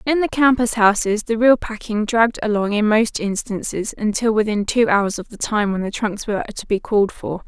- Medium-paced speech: No, fast, 215 wpm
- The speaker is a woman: Yes, female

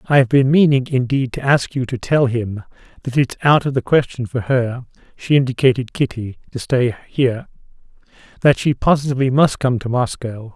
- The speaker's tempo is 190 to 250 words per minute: No, average, 175 wpm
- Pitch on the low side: Yes, low, 130 Hz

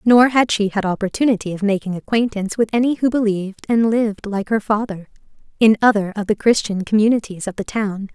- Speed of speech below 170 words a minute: No, average, 190 wpm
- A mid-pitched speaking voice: No, high, 210 Hz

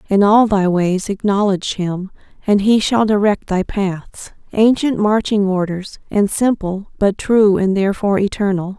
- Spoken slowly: No, average, 150 wpm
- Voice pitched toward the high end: Yes, high, 200 Hz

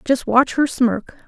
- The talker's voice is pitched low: No, very high, 250 Hz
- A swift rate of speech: No, average, 190 wpm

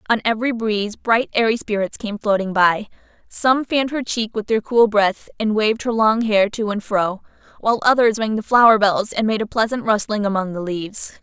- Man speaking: No, female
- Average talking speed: No, fast, 210 wpm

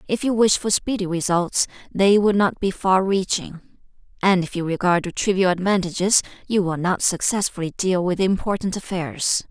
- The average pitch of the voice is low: No, high, 190 Hz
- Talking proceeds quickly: No, average, 165 wpm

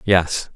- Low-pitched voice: Yes, very low, 90 Hz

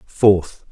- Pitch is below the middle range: Yes, low, 100 Hz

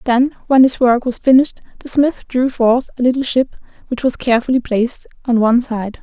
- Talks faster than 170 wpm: Yes, average, 200 wpm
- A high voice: Yes, very high, 250 Hz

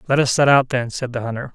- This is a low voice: Yes, low, 130 Hz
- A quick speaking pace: Yes, fast, 310 wpm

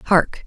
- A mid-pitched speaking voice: Yes, medium, 180 Hz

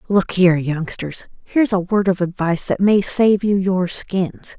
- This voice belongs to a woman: Yes, female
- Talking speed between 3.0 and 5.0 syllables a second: Yes, 4.7 syllables/s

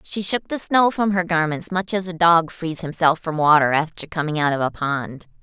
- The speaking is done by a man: No, female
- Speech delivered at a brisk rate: Yes, fast, 230 wpm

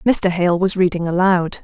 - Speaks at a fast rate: No, average, 185 wpm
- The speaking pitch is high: No, medium, 180 Hz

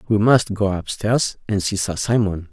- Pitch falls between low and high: No, low, 100 Hz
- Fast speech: No, average, 190 wpm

